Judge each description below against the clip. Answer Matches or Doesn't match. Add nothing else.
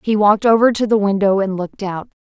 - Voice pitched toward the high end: Matches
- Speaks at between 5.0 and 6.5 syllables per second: Matches